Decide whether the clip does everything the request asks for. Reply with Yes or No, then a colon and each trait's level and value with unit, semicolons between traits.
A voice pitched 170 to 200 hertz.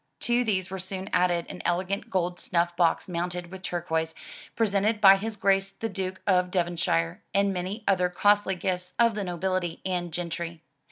Yes: medium, 185 Hz